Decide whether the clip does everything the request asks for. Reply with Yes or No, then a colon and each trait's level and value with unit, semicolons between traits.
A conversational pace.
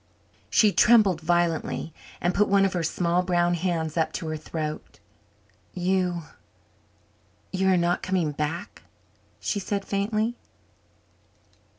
No: slow, 120 wpm